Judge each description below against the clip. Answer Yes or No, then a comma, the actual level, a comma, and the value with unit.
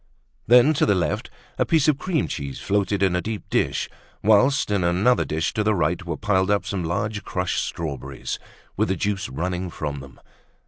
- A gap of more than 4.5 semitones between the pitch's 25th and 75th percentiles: No, average, 3.7 semitones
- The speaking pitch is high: No, very low, 95 Hz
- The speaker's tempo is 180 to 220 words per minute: Yes, average, 190 wpm